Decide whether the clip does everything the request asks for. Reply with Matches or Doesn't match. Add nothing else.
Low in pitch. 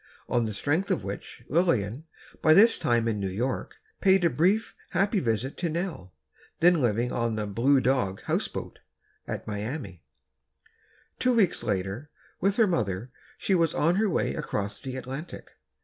Matches